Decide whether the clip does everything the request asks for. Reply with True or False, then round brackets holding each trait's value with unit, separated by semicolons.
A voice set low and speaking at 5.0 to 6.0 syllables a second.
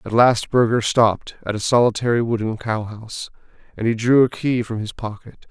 True (115 Hz; 5.4 syllables/s)